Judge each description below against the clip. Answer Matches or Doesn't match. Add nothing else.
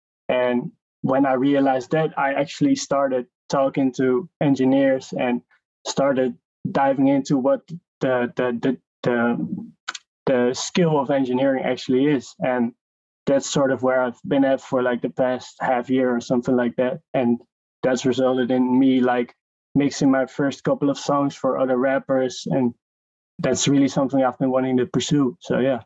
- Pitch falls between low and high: Doesn't match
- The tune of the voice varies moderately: Doesn't match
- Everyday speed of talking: Matches